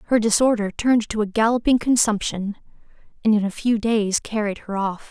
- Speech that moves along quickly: No, average, 175 wpm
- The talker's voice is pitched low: No, high, 215 Hz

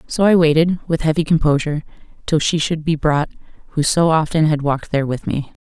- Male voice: No, female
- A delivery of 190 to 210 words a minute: Yes, average, 200 wpm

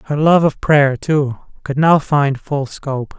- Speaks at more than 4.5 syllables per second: No, 4.0 syllables/s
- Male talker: Yes, male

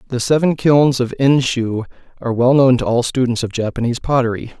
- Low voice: Yes, low, 125 Hz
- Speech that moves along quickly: No, average, 185 wpm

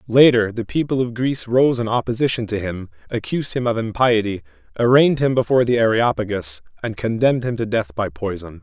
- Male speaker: Yes, male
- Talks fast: No, average, 180 wpm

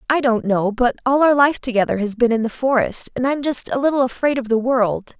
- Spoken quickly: Yes, fast, 255 wpm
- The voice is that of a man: No, female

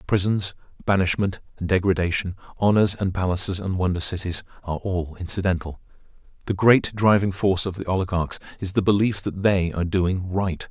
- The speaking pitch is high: No, very low, 95 Hz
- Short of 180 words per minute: Yes, average, 155 wpm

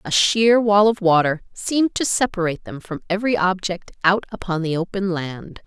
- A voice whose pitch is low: No, high, 190 Hz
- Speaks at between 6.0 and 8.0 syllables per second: No, 5.2 syllables/s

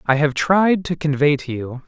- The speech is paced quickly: Yes, fast, 225 wpm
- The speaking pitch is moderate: Yes, medium, 150 Hz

